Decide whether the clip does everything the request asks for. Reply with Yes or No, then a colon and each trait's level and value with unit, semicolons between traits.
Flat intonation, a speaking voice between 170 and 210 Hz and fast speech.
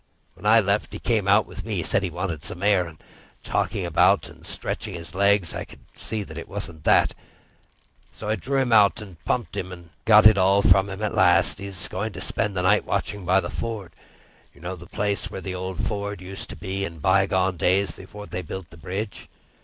No: narrow, 2.3 semitones; very low, 95 Hz; fast, 220 wpm